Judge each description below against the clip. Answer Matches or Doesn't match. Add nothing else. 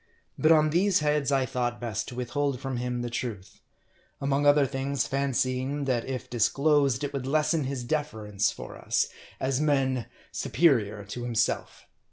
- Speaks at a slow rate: Doesn't match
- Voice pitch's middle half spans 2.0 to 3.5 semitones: Matches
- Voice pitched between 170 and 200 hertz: Doesn't match